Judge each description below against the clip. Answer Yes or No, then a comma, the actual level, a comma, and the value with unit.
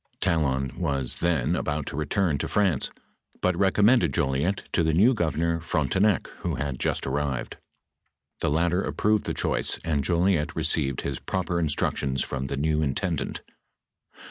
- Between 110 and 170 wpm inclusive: Yes, average, 150 wpm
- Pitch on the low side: Yes, very low, 80 Hz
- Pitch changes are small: No, average, 4.2 semitones